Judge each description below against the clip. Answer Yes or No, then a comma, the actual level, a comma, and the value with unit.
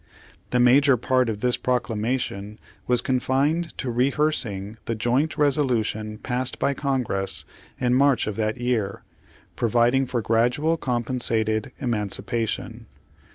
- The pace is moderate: No, slow, 120 wpm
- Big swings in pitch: No, average, 3.0 semitones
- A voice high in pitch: No, low, 125 Hz